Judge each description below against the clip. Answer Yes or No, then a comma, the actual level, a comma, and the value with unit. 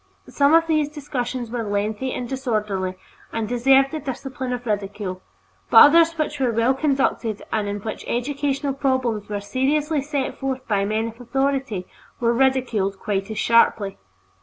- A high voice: Yes, very high, 250 Hz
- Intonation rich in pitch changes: No, average, 4.2 semitones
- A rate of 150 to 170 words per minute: Yes, average, 160 wpm